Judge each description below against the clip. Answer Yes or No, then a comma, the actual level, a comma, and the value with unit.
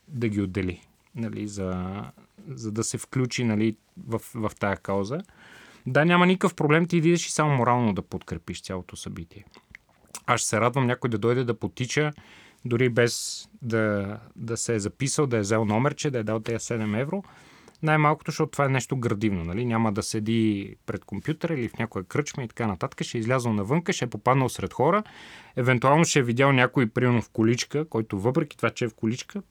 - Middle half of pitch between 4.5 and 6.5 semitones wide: Yes, average, 5.0 semitones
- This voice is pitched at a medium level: No, low, 120 Hz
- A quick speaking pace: Yes, fast, 195 wpm